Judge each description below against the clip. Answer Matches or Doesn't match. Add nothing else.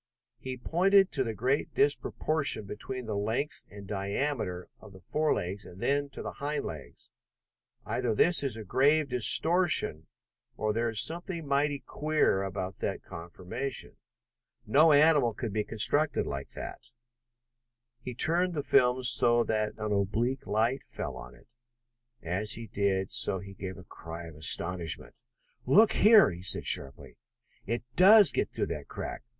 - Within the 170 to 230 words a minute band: Doesn't match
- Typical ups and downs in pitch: Doesn't match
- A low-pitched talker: Matches